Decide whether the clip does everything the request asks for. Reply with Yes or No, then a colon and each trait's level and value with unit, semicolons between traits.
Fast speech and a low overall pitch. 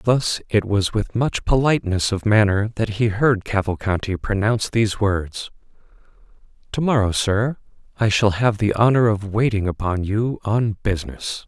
No: average, 150 wpm; low, 105 Hz